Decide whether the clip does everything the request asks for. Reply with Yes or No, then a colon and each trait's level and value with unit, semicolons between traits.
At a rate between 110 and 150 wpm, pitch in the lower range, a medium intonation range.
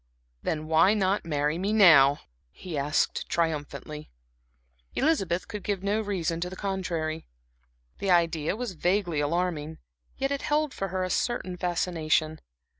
No: average, 145 wpm; medium, 175 Hz; average, 3.8 semitones